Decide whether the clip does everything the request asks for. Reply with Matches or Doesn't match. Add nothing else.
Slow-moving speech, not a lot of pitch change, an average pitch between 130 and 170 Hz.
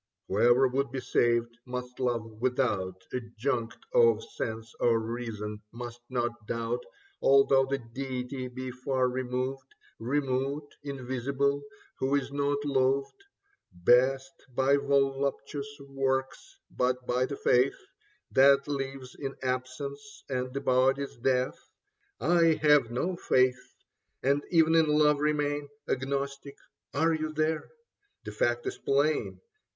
Matches